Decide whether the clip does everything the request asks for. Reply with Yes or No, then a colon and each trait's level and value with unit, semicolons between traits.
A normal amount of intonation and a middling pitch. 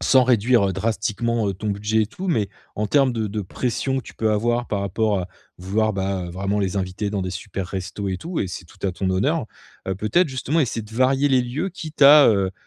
No: average, 4.7 semitones; low, 110 Hz